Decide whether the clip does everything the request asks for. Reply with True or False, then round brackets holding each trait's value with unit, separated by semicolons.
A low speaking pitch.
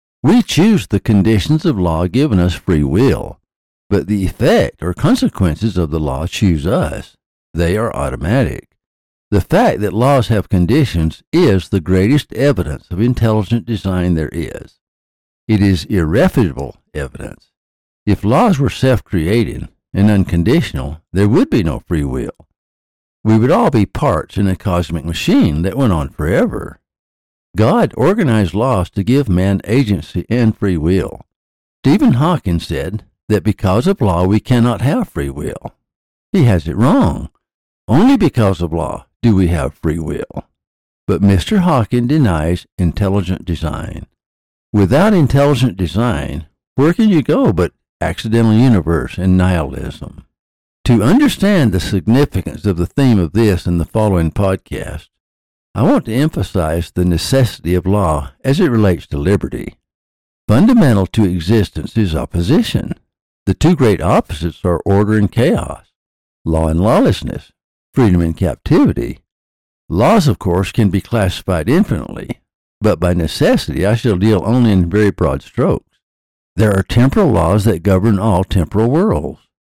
True (95 Hz)